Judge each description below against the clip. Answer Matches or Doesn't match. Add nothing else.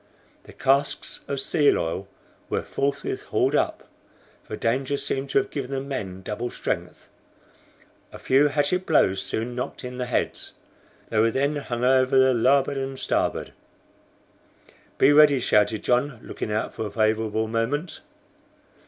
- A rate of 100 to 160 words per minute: Matches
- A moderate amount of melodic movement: Matches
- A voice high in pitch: Doesn't match